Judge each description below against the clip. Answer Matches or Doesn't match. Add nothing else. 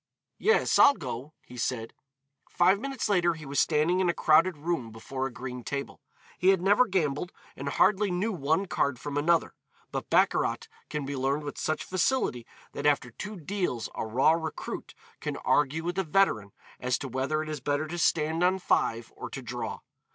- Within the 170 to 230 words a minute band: Matches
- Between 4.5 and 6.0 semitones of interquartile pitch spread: Matches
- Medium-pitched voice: Matches